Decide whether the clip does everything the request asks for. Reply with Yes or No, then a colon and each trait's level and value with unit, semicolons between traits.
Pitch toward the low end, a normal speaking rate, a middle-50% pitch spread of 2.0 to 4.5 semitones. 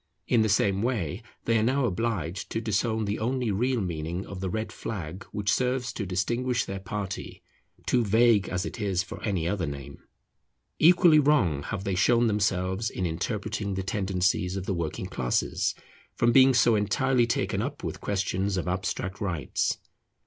Yes: low, 100 Hz; average, 170 wpm; average, 4.1 semitones